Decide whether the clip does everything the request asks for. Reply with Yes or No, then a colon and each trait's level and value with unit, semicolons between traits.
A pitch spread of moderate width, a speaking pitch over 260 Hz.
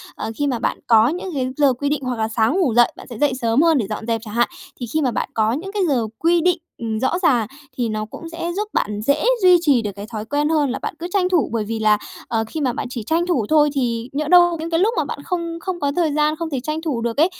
No: wide, 6.2 semitones; very high, 280 Hz